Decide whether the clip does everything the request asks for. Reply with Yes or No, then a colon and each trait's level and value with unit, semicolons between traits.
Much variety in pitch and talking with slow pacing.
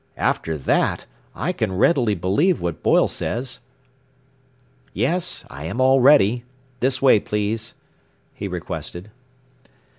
Yes: wide, 6.3 semitones; slow, 115 wpm